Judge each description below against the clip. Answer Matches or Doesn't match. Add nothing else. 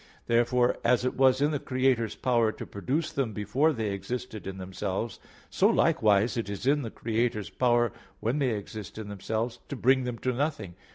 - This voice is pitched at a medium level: Doesn't match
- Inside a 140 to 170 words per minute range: Doesn't match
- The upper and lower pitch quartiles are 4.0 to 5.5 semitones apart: Doesn't match